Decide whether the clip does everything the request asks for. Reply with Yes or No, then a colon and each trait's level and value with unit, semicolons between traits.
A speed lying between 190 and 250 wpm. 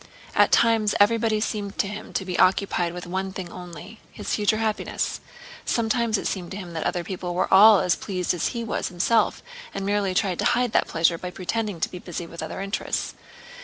Yes: average, 200 wpm